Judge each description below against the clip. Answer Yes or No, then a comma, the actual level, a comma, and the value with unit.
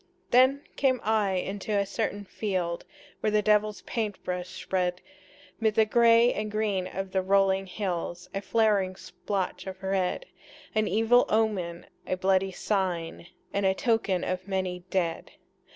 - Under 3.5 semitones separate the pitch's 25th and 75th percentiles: Yes, narrow, 2.6 semitones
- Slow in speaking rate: No, average, 150 wpm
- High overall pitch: Yes, high, 195 Hz